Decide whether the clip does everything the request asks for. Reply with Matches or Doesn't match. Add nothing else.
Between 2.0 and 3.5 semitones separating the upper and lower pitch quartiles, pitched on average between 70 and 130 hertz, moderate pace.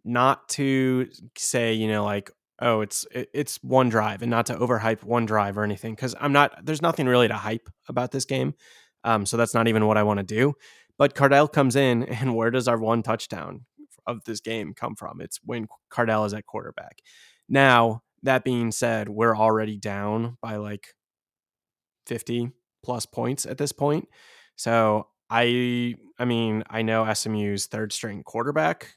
Matches